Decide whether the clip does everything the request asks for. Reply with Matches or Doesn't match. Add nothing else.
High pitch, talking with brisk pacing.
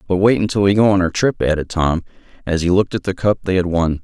Doesn't match